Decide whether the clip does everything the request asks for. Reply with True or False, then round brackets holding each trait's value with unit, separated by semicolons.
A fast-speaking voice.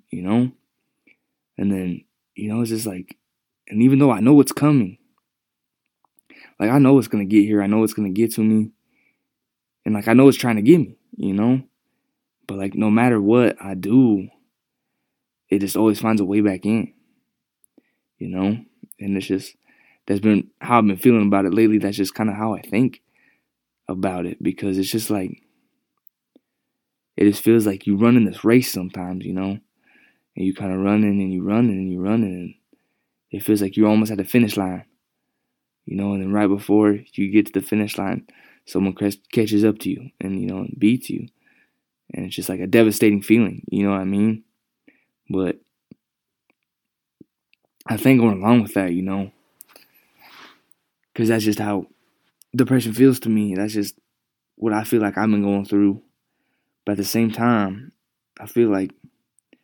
False (185 wpm)